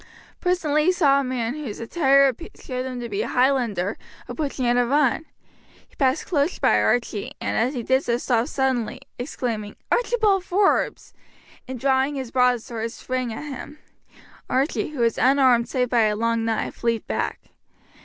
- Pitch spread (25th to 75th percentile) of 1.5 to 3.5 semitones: Yes, average, 3.2 semitones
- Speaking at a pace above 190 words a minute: No, average, 165 wpm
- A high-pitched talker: Yes, very high, 255 Hz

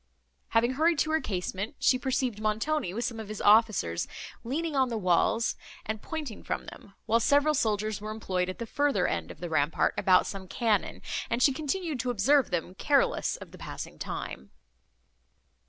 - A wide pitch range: Yes, wide, 5.8 semitones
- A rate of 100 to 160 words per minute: No, average, 180 wpm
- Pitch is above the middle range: Yes, high, 225 Hz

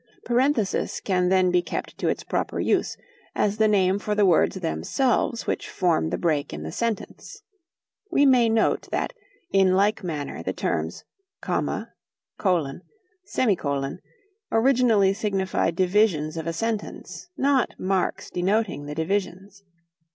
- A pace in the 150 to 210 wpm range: No, slow, 135 wpm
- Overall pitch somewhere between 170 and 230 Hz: Yes, high, 190 Hz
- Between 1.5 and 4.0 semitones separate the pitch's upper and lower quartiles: No, average, 4.6 semitones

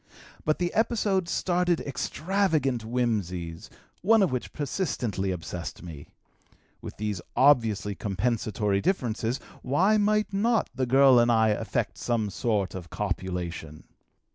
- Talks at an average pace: No, slow, 120 wpm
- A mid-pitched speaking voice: No, low, 120 Hz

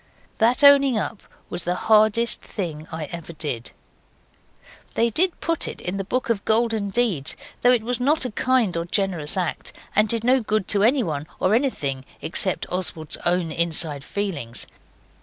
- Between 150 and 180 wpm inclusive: Yes, average, 165 wpm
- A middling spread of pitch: No, wide, 6.0 semitones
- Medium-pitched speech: No, high, 200 Hz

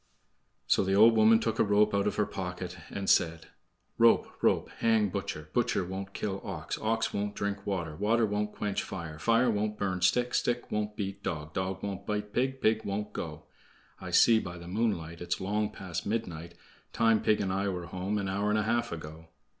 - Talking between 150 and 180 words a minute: No, average, 200 wpm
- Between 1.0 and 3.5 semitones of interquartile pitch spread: Yes, average, 3.0 semitones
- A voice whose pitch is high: No, low, 100 Hz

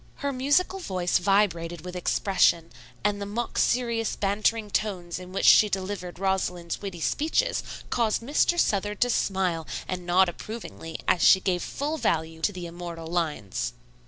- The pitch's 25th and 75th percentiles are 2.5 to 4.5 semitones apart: Yes, average, 3.7 semitones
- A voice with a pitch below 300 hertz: Yes, high, 190 Hz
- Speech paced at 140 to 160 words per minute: Yes, average, 155 wpm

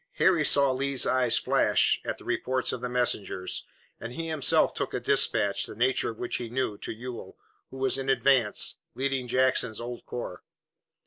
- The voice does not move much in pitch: Yes, narrow, 2.2 semitones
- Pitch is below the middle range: Yes, low, 125 Hz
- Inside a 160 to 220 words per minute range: Yes, average, 180 wpm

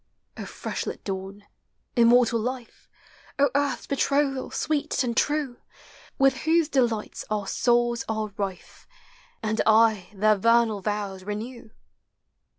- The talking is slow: Yes, slow, 120 wpm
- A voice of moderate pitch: No, high, 230 Hz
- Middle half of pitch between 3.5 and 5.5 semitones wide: Yes, average, 3.9 semitones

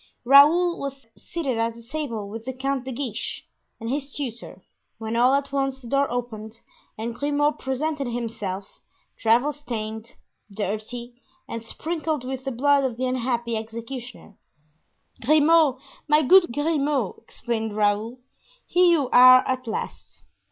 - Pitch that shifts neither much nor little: Yes, average, 3.7 semitones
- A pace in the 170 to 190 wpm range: No, slow, 135 wpm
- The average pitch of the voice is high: Yes, very high, 255 Hz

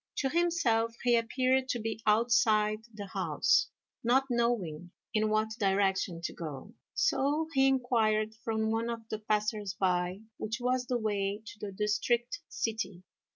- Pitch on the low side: No, high, 220 Hz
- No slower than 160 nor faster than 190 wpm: No, average, 150 wpm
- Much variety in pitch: No, average, 2.7 semitones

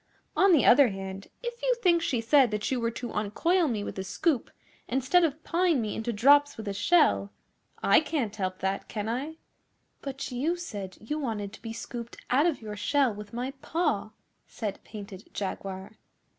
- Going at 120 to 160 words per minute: No, average, 185 wpm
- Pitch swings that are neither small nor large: No, wide, 6.4 semitones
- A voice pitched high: Yes, high, 240 Hz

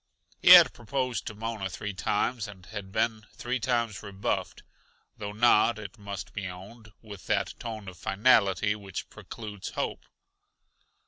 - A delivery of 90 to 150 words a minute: Yes, average, 145 wpm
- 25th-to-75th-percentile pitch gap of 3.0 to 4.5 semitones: No, narrow, 2.5 semitones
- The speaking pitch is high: No, low, 105 Hz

